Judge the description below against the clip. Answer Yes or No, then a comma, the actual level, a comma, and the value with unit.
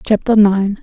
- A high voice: Yes, high, 205 Hz